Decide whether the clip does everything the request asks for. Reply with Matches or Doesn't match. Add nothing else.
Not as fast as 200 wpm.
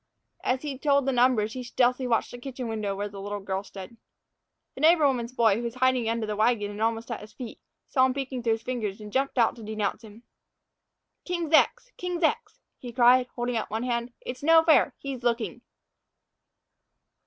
Doesn't match